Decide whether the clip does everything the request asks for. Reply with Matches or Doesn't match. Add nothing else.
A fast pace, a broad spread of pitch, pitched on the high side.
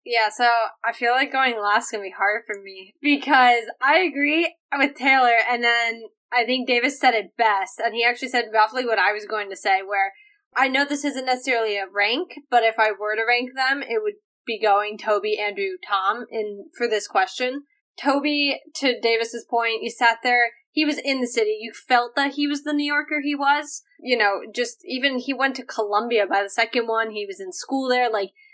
Doesn't match